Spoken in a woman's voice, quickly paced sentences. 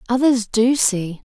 No: female; average, 140 wpm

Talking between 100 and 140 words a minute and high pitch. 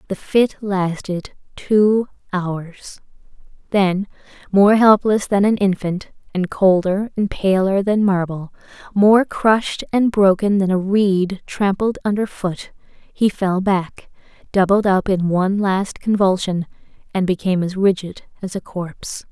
Yes: slow, 135 wpm; high, 195 Hz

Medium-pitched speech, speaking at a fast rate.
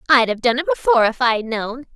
No: very high, 250 Hz; fast, 245 wpm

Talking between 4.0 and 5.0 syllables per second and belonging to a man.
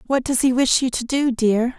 No: 4.9 syllables/s; female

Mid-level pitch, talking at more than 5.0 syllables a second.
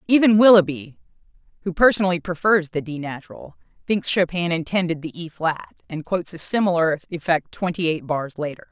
Yes: medium, 175 Hz; 5.5 syllables/s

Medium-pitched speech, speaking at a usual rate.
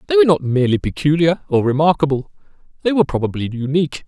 Yes: medium, 155 Hz; average, 160 wpm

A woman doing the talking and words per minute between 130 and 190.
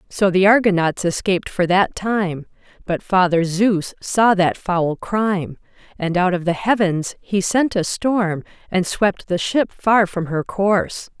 Yes: female; average, 165 wpm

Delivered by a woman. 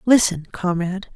Yes: female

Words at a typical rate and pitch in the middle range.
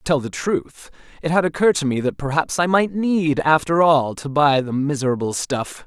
No: fast, 215 wpm; medium, 150 Hz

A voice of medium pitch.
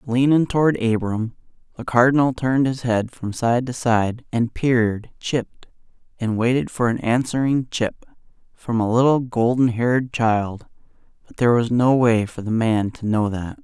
No: low, 120 Hz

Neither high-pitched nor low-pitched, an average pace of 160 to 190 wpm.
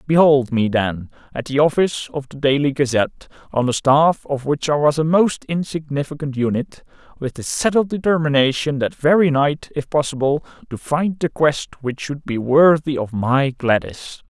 Yes: medium, 145 Hz; average, 170 wpm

